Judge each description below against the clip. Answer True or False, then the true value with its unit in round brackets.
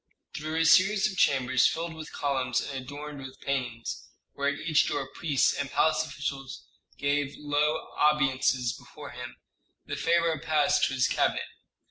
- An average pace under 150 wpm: False (155 wpm)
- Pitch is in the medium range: True (145 Hz)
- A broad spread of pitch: False (2.7 semitones)